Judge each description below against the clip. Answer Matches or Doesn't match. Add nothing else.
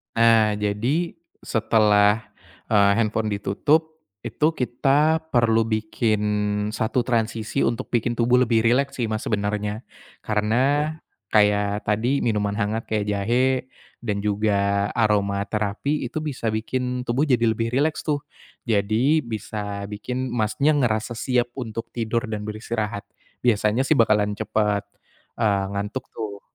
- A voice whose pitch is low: Matches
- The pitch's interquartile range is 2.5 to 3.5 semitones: Matches